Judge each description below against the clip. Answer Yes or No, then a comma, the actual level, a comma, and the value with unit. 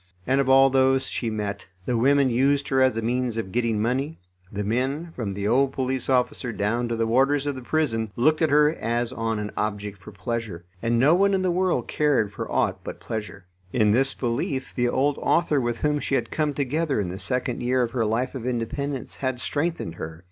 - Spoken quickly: Yes, fast, 220 wpm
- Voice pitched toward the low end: Yes, low, 125 Hz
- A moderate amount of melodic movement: Yes, average, 3.6 semitones